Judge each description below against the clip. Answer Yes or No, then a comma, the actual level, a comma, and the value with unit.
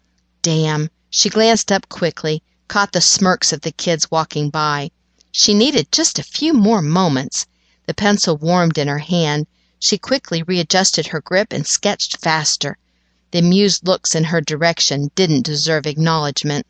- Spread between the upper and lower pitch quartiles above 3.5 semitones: Yes, average, 4.0 semitones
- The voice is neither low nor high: Yes, medium, 165 Hz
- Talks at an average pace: Yes, average, 155 wpm